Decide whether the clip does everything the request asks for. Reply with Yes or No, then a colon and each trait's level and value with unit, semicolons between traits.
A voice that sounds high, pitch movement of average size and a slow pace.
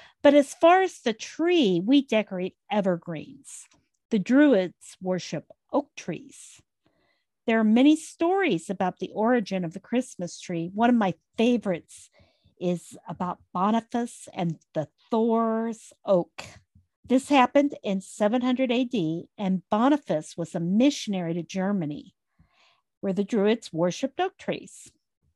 No: high, 210 Hz; wide, 6.0 semitones; slow, 130 wpm